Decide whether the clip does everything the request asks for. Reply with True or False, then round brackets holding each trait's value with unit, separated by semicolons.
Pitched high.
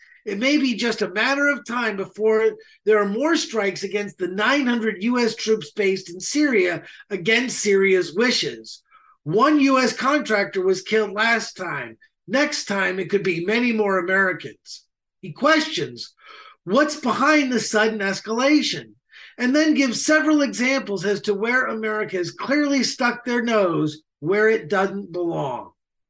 True (220 Hz)